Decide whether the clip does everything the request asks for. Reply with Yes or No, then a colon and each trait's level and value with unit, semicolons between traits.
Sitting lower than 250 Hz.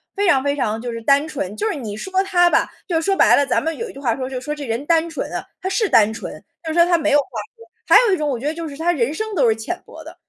No: very high, 300 Hz